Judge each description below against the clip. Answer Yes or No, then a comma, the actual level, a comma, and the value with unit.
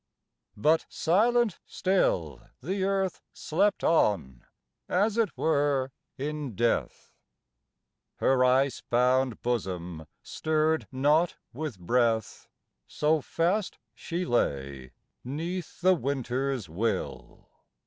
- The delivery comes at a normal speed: No, slow, 95 wpm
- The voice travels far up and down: Yes, wide, 6.4 semitones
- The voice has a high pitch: No, medium, 140 Hz